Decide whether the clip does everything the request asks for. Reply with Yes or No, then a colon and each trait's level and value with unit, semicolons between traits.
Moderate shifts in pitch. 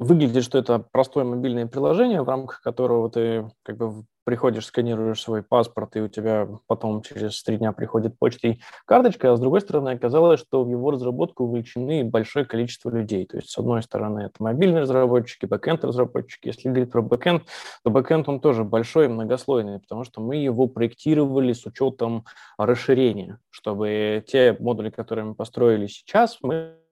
Yes: average, 3.0 semitones